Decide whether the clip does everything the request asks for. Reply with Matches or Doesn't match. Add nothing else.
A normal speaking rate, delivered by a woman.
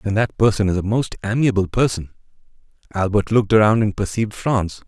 Doesn't match